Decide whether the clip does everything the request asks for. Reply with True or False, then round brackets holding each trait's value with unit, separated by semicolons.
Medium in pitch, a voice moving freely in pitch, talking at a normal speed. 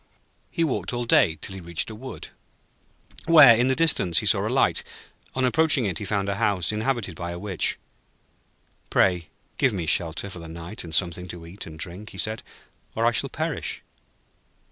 False (100 Hz; 5.7 semitones; 190 wpm)